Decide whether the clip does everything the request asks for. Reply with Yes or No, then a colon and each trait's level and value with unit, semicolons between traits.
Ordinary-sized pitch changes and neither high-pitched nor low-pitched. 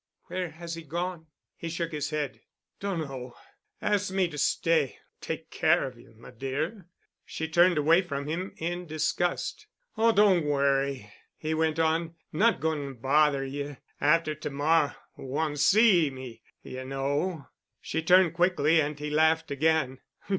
Yes: average, 3.2 semitones; medium, 155 Hz